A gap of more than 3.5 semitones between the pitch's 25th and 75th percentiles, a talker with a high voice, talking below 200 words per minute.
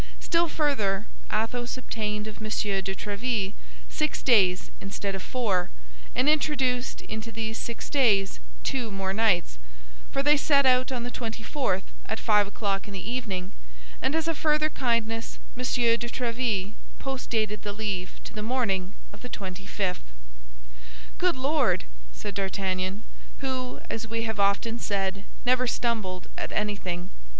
Yes: average, 4.3 semitones; high, 220 Hz; average, 150 wpm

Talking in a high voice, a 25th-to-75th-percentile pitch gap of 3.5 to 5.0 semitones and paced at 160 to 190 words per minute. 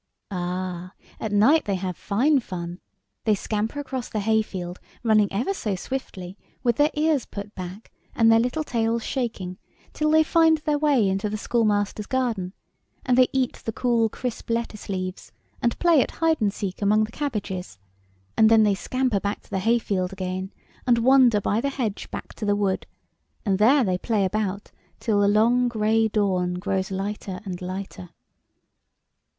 Yes: high, 215 Hz; average, 4.1 semitones; average, 170 wpm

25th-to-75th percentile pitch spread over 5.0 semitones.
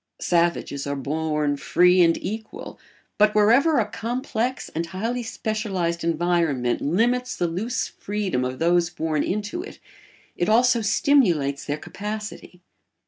Yes: wide, 5.4 semitones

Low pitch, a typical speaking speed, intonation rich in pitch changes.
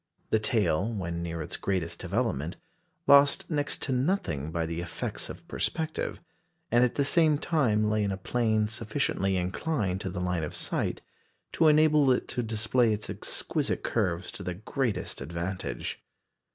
Yes: low, 105 Hz; average, 160 wpm; wide, 6.5 semitones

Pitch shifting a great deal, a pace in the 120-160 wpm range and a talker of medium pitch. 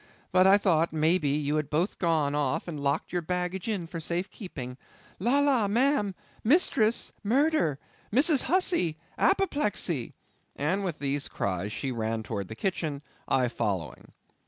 Yes: wide, 6.6 semitones; average, 145 wpm; medium, 170 Hz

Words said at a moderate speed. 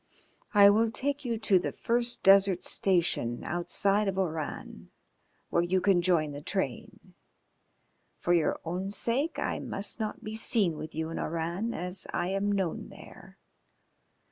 Yes: average, 150 wpm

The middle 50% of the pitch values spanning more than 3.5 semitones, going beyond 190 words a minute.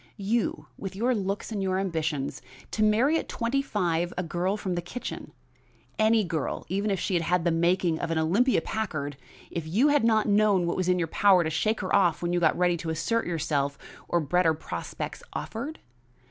Yes: average, 4.4 semitones; average, 200 wpm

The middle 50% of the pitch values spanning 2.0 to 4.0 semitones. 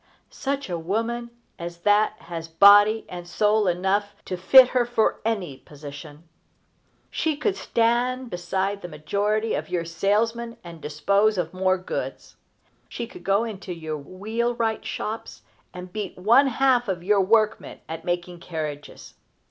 No: average, 4.6 semitones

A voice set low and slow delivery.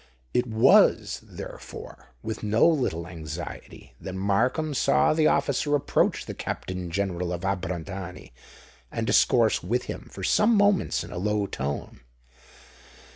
Yes: low, 100 Hz; slow, 130 wpm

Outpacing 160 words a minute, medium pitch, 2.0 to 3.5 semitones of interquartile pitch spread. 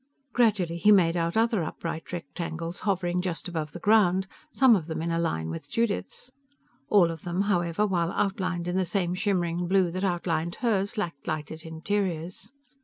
Yes: average, 175 wpm; medium, 175 Hz; average, 3.0 semitones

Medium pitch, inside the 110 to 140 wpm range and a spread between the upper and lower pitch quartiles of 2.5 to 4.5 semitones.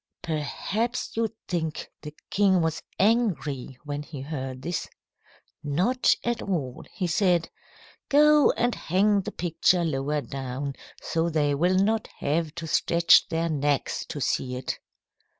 No: medium, 165 Hz; slow, 135 wpm; average, 5.2 semitones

